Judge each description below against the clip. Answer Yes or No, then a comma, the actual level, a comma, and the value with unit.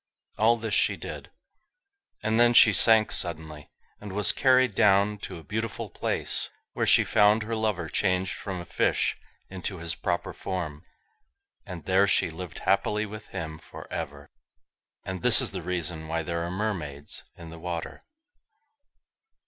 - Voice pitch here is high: No, very low, 95 Hz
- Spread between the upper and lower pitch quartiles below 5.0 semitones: Yes, average, 4.2 semitones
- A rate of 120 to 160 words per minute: Yes, average, 155 wpm